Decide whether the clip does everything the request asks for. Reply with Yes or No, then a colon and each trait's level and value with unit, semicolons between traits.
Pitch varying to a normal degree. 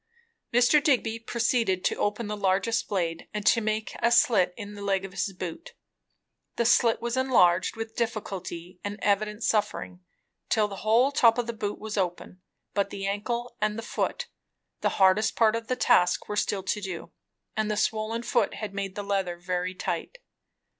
Yes: average, 3.0 semitones